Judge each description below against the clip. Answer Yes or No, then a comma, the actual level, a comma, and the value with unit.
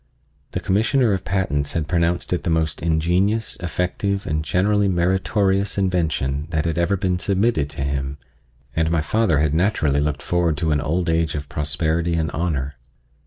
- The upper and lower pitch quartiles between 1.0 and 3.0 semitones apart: No, average, 3.9 semitones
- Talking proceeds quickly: No, average, 165 wpm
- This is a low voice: Yes, very low, 85 Hz